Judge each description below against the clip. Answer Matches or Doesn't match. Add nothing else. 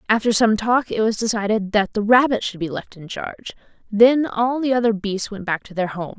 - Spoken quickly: Matches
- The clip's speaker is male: Doesn't match